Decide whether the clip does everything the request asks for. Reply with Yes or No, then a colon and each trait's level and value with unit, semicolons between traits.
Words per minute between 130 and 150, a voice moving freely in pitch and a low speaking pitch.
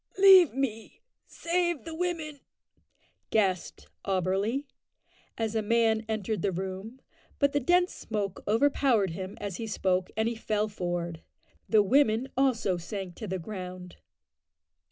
No: slow, 135 wpm; wide, 6.1 semitones; high, 220 Hz